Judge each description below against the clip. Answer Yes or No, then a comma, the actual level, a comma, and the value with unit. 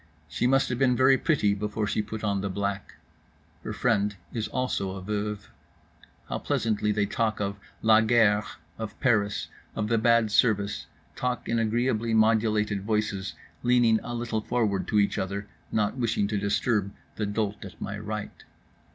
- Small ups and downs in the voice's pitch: Yes, narrow, 2.2 semitones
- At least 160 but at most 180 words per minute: Yes, average, 165 wpm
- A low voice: Yes, low, 105 Hz